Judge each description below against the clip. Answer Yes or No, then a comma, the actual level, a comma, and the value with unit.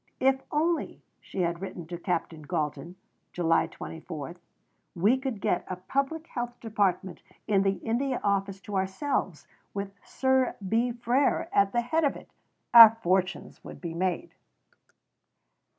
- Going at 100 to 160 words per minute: Yes, average, 140 wpm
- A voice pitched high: Yes, high, 200 Hz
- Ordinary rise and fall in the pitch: No, wide, 5.8 semitones